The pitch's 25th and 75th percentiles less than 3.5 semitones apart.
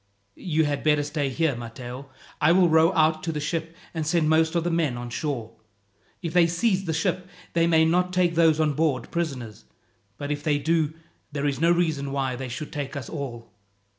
Yes: average, 3.0 semitones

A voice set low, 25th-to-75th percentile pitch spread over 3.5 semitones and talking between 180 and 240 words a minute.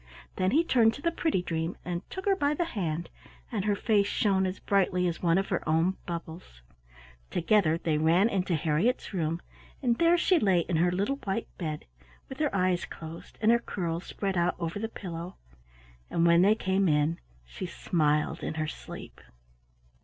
No: medium, 180 Hz; average, 4.4 semitones; average, 185 wpm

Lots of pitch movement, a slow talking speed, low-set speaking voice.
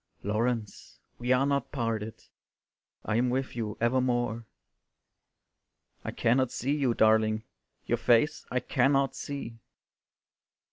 No: narrow, 2.6 semitones; slow, 110 wpm; low, 120 Hz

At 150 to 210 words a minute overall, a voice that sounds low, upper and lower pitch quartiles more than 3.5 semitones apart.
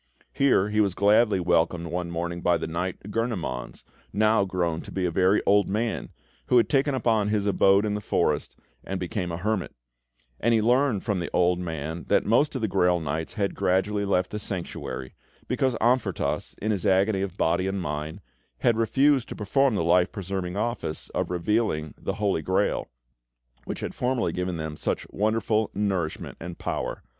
Yes: average, 180 wpm; very low, 95 Hz; average, 3.9 semitones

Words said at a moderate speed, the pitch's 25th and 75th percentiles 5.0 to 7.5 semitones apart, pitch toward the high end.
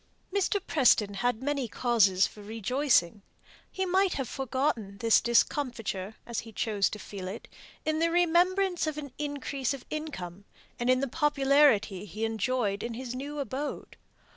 Yes: average, 155 wpm; wide, 5.6 semitones; very high, 255 Hz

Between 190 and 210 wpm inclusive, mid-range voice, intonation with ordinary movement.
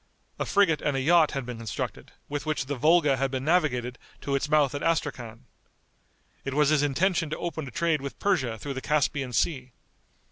Yes: average, 200 wpm; medium, 145 Hz; average, 3.1 semitones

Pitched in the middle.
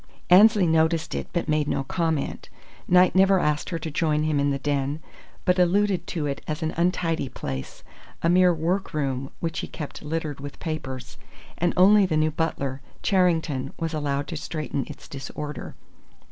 Yes: medium, 160 Hz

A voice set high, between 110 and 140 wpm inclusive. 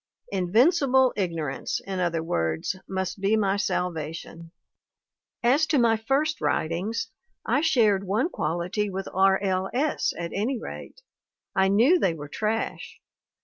Yes: high, 195 Hz; slow, 135 wpm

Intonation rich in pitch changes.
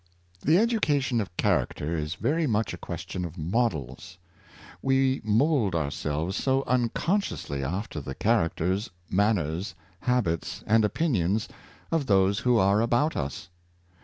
Yes: wide, 7.1 semitones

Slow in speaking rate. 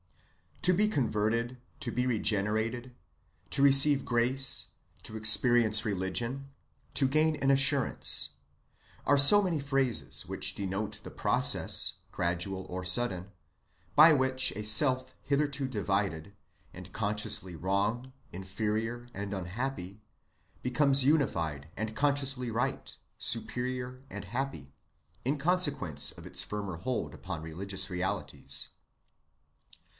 Yes: slow, 110 wpm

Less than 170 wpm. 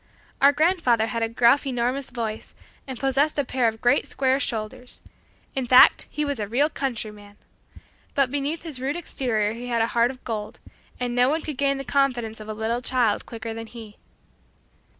No: average, 190 wpm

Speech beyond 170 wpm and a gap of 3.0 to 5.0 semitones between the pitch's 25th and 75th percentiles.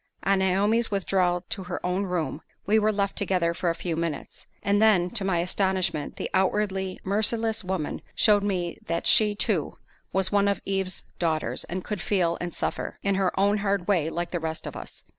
No: average, 195 wpm; narrow, 2.5 semitones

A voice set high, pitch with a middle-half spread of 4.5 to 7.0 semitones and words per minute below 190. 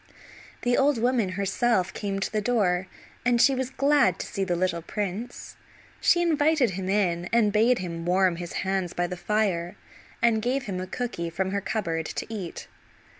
Yes: high, 200 Hz; average, 5.1 semitones; average, 180 wpm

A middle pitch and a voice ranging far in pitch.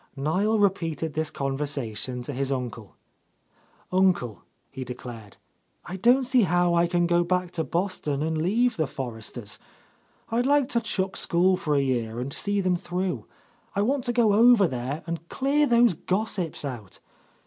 Yes: medium, 175 Hz; wide, 6.8 semitones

